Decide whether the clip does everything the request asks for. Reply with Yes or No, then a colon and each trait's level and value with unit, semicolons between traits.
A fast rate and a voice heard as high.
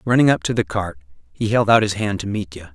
No: fast, 260 wpm; low, 100 Hz